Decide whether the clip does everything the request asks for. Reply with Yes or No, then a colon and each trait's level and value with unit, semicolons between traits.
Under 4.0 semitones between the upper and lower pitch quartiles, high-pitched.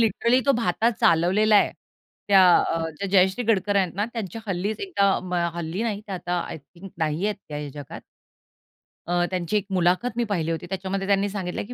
Yes: average, 3.1 semitones; high, 195 Hz